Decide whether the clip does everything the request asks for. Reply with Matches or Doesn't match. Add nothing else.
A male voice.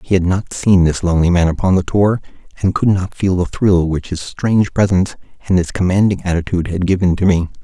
Matches